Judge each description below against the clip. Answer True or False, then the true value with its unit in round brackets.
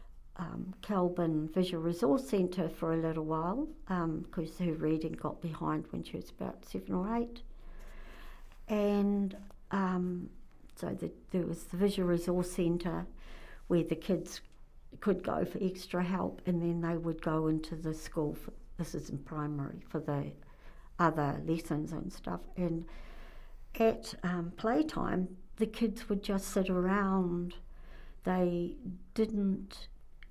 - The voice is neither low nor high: True (175 Hz)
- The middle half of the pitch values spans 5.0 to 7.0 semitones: False (2.9 semitones)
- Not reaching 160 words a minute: True (140 wpm)